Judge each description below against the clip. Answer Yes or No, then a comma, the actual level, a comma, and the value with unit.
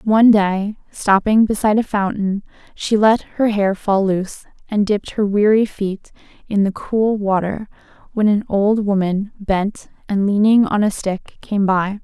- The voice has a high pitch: Yes, high, 205 Hz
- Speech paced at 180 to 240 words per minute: No, average, 165 wpm